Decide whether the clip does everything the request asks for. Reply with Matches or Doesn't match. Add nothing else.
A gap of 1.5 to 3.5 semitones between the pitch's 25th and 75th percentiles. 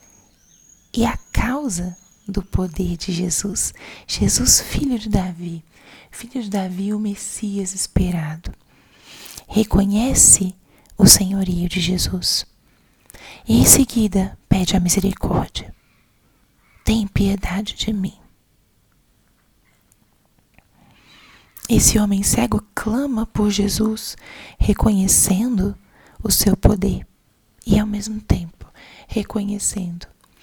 Matches